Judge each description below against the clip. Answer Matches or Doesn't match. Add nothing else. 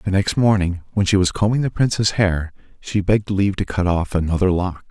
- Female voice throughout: Doesn't match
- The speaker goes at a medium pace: Doesn't match